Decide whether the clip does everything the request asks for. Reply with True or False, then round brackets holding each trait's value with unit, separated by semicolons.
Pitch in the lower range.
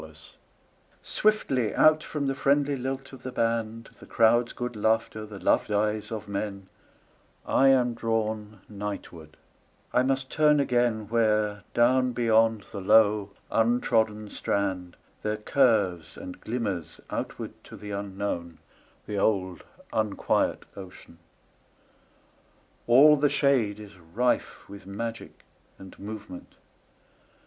True (110 Hz)